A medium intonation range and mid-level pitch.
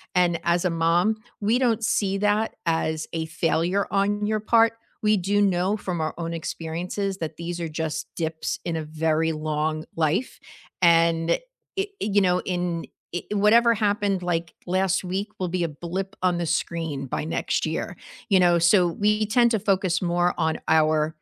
Yes: average, 3.5 semitones; medium, 175 Hz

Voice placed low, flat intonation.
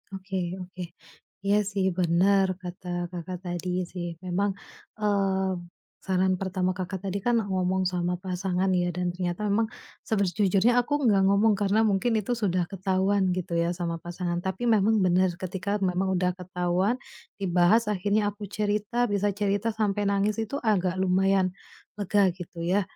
No: high, 190 Hz; narrow, 2.2 semitones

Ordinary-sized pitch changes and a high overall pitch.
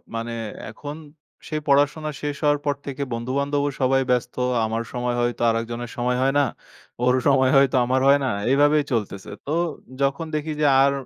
No: average, 3.0 semitones; low, 135 Hz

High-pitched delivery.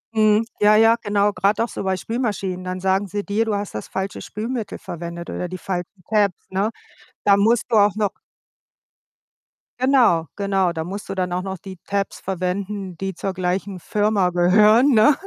Yes: high, 200 Hz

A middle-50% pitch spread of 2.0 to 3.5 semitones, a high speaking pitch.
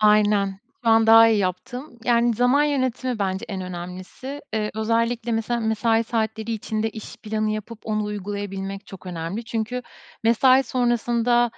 Yes: narrow, 2.5 semitones; high, 220 Hz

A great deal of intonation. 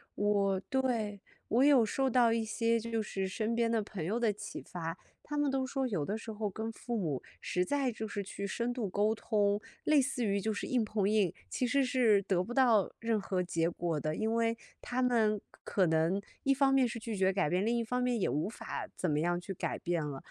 No: average, 3.8 semitones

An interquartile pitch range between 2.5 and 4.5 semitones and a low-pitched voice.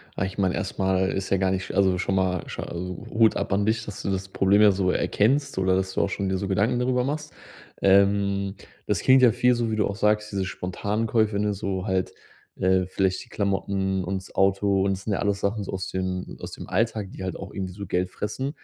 No: narrow, 2.0 semitones; low, 100 Hz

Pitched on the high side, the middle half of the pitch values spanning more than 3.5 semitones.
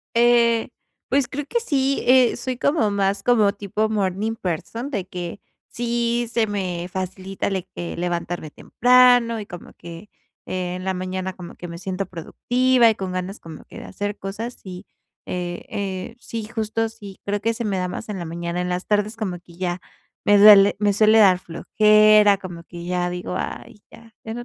Yes: high, 200 Hz; average, 3.9 semitones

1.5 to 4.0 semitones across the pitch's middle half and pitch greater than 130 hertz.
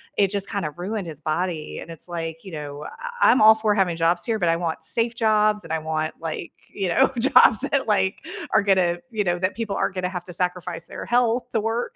No: average, 4.7 semitones; high, 190 Hz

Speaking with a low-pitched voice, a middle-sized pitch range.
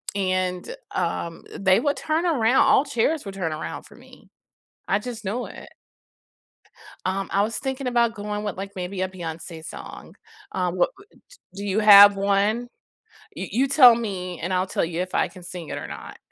No: high, 200 Hz; average, 4.2 semitones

